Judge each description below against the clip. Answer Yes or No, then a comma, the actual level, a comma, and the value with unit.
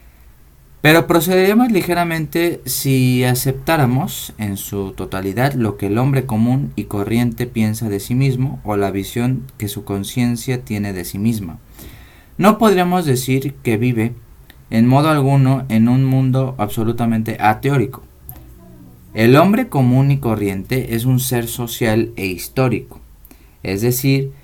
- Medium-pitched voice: No, low, 120 Hz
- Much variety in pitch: No, average, 4.4 semitones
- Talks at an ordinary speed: Yes, average, 135 wpm